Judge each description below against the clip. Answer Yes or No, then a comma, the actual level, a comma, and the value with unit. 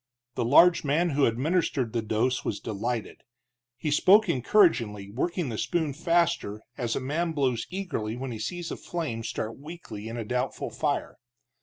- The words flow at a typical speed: Yes, average, 165 wpm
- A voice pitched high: No, low, 130 Hz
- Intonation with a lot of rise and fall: Yes, wide, 6.8 semitones